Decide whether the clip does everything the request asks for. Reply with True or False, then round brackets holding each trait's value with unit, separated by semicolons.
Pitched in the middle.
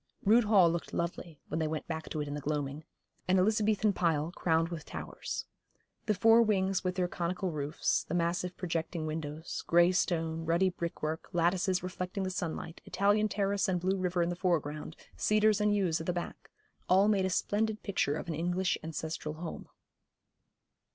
True (175 Hz)